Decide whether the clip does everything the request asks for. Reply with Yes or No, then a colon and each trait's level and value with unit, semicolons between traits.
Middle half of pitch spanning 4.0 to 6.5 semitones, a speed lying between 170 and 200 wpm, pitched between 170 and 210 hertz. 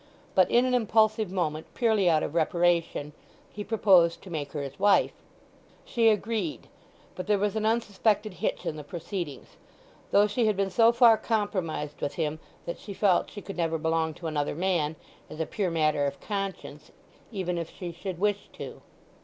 Yes: average, 4.5 semitones; average, 180 wpm; medium, 185 Hz